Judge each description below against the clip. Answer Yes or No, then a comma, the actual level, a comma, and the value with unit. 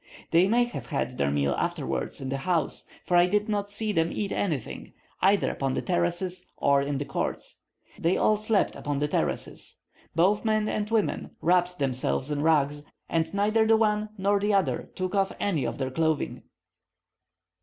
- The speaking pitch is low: No, medium, 180 Hz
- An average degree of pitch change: No, wide, 5.9 semitones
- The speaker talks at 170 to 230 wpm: Yes, average, 180 wpm